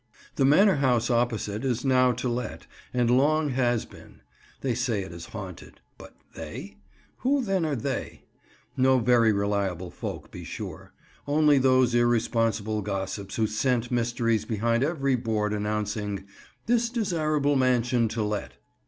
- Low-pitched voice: Yes, low, 120 Hz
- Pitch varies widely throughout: No, average, 3.8 semitones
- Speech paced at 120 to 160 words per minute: Yes, average, 140 wpm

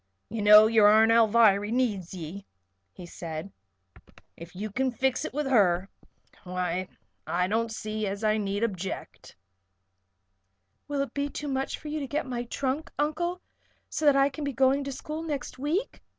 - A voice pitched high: Yes, high, 230 Hz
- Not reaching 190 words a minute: Yes, average, 175 wpm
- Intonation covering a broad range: Yes, wide, 5.7 semitones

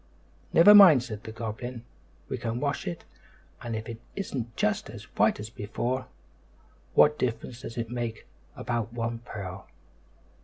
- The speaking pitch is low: Yes, low, 115 Hz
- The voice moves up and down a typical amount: No, narrow, 2.2 semitones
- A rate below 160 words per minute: Yes, average, 150 wpm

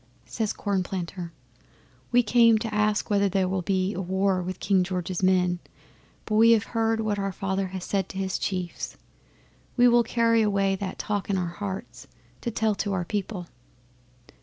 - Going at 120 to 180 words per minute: Yes, average, 170 wpm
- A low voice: No, high, 195 Hz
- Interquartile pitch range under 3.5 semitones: Yes, narrow, 2.5 semitones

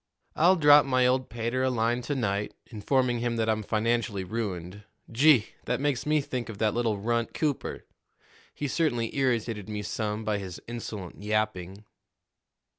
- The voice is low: Yes, low, 115 Hz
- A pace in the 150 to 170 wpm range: Yes, average, 160 wpm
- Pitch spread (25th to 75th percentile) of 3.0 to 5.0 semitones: Yes, average, 3.4 semitones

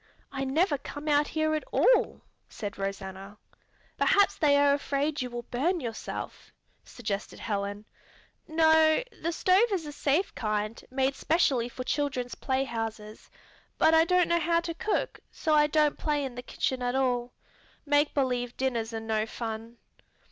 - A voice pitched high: Yes, very high, 270 Hz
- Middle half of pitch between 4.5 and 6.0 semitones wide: Yes, average, 5.1 semitones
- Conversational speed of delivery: Yes, average, 155 wpm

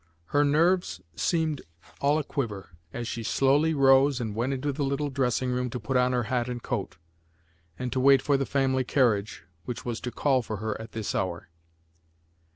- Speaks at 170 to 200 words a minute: Yes, average, 185 wpm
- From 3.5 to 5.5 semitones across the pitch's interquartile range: No, average, 3.0 semitones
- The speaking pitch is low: Yes, low, 130 Hz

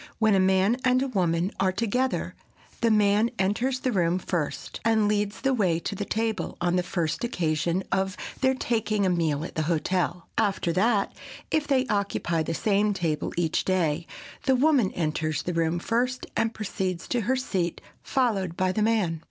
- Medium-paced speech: Yes, average, 180 wpm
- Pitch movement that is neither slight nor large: Yes, average, 4.7 semitones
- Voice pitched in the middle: No, high, 195 Hz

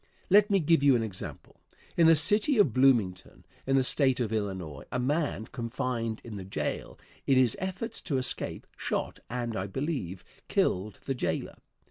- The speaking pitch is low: Yes, low, 125 Hz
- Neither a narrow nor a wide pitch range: No, wide, 5.8 semitones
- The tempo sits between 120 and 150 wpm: No, average, 170 wpm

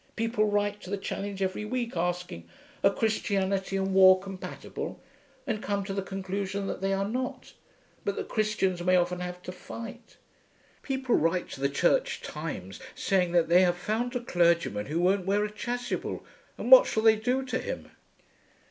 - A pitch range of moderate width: Yes, average, 3.3 semitones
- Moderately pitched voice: No, high, 195 Hz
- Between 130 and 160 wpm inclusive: No, average, 175 wpm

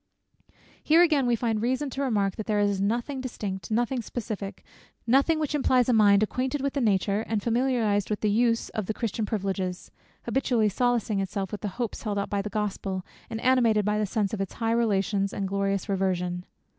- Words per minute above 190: Yes, average, 200 wpm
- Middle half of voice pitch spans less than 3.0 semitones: No, average, 3.5 semitones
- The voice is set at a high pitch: Yes, high, 215 Hz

